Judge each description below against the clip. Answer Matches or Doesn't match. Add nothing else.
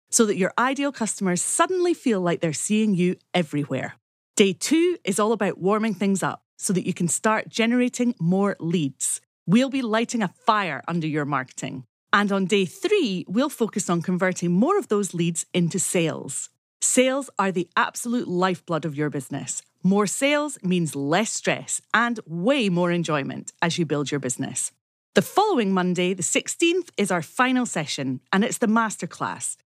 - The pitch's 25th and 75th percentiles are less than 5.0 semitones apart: Doesn't match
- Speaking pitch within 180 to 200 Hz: Matches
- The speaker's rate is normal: Matches